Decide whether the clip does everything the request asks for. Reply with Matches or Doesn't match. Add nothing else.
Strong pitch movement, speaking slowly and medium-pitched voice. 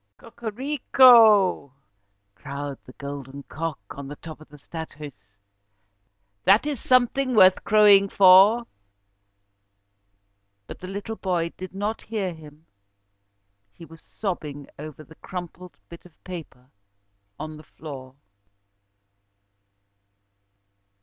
Matches